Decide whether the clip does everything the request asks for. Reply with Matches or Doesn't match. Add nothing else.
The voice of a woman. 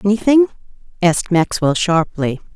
Matches